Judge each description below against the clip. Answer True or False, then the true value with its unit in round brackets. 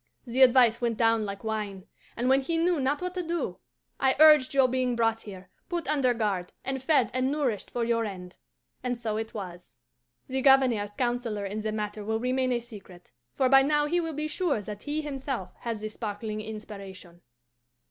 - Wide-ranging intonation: False (4.2 semitones)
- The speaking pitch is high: True (240 Hz)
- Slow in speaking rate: False (195 wpm)